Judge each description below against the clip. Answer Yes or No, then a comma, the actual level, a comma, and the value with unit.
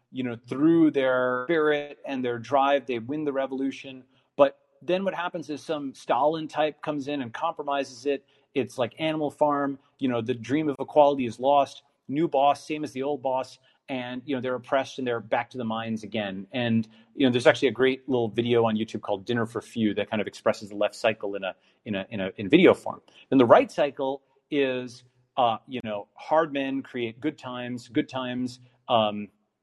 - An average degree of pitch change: Yes, average, 3.4 semitones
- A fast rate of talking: Yes, fast, 210 wpm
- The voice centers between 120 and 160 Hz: Yes, low, 130 Hz